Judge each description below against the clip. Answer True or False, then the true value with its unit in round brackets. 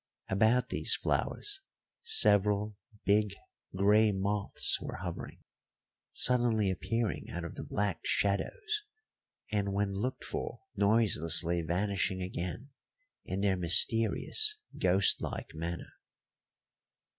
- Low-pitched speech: True (100 Hz)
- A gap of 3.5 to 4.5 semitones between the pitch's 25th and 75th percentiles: False (3.0 semitones)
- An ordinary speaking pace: False (100 wpm)